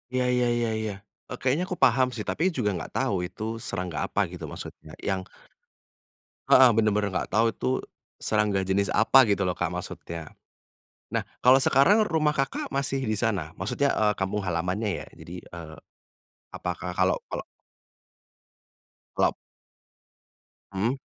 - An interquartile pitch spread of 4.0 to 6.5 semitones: Yes, average, 5.1 semitones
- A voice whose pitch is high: No, low, 110 Hz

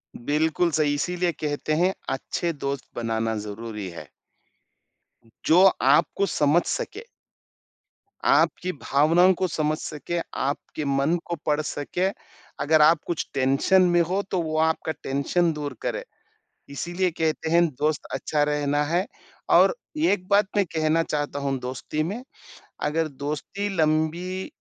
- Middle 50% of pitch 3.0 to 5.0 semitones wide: Yes, average, 3.3 semitones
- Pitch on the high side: No, medium, 155 Hz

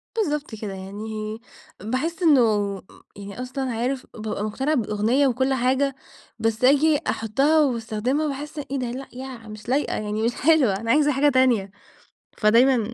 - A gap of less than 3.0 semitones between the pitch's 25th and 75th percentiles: No, average, 4.2 semitones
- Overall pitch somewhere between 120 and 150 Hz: No, very high, 250 Hz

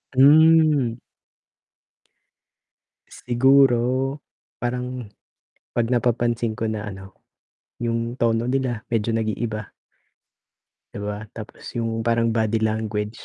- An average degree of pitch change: No, narrow, 2.3 semitones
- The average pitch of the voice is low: Yes, low, 115 Hz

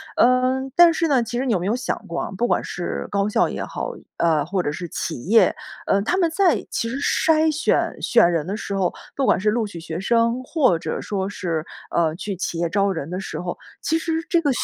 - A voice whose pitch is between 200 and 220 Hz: Yes, high, 205 Hz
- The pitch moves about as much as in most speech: No, wide, 7.1 semitones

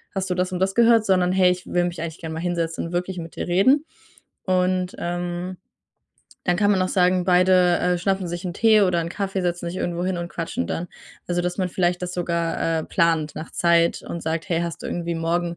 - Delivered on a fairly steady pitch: Yes, narrow, 1.4 semitones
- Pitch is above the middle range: No, medium, 175 Hz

